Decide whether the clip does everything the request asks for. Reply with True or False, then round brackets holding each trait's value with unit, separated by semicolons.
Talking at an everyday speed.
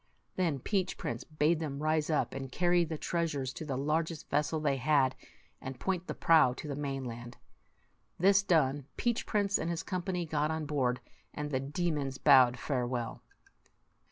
True (170 wpm)